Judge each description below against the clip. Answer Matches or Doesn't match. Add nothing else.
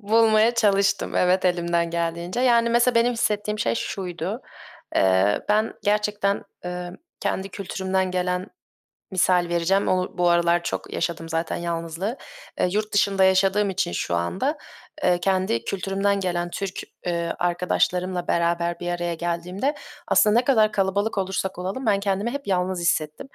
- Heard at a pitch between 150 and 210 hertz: Matches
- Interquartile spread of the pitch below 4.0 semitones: Matches